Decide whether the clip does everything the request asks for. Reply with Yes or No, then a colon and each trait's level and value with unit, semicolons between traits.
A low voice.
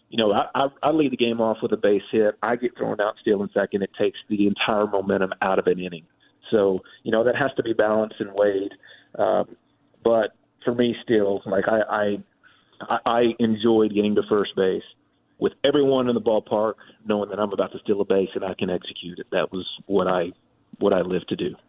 Yes: low, 105 Hz